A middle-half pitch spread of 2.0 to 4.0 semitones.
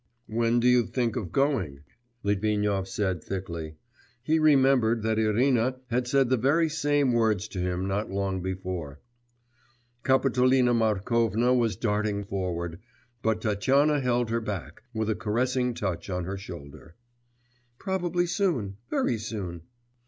No: average, 4.8 semitones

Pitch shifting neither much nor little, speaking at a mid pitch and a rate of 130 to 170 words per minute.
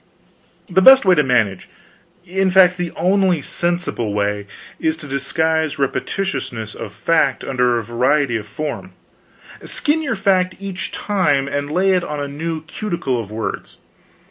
No: wide, 6.5 semitones; medium, 155 Hz; average, 145 wpm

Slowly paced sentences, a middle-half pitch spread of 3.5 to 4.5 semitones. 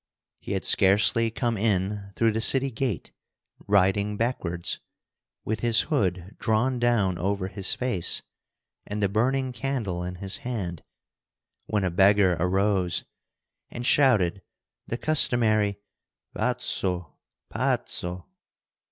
Yes: slow, 110 wpm; average, 4.0 semitones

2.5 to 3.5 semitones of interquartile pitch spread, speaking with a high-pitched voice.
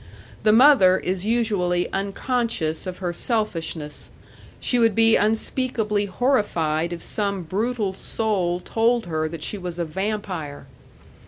No: average, 4.5 semitones; high, 195 Hz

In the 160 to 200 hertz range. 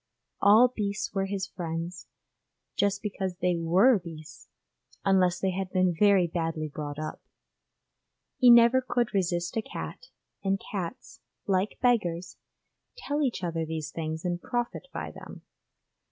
Yes: medium, 185 Hz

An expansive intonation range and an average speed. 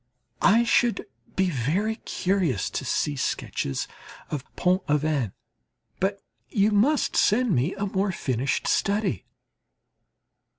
No: wide, 6.3 semitones; slow, 115 wpm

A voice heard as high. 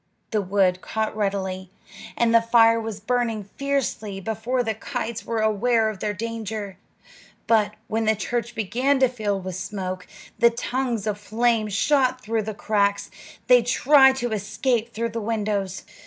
Yes: high, 220 Hz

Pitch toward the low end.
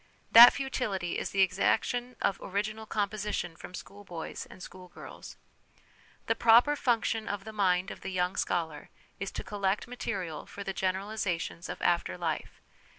No: high, 195 Hz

